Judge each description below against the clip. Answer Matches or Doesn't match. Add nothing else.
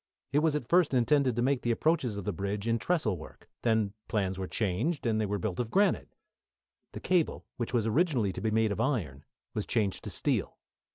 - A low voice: Matches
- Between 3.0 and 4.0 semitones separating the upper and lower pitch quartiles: Doesn't match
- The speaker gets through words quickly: Matches